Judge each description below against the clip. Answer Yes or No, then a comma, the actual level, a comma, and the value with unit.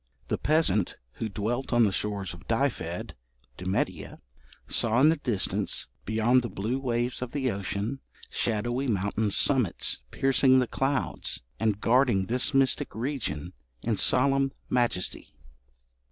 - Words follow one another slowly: Yes, slow, 130 wpm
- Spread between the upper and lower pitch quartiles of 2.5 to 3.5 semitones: No, average, 4.5 semitones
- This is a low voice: Yes, low, 120 Hz